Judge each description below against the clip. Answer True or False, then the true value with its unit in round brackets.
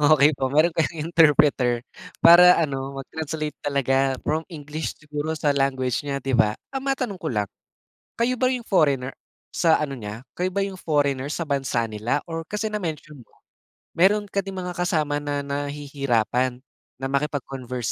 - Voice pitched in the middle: True (145 Hz)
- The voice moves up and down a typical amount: True (3.8 semitones)